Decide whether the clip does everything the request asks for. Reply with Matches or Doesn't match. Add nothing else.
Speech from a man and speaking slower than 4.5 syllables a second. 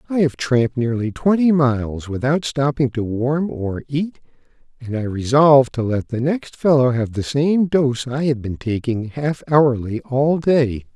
Matches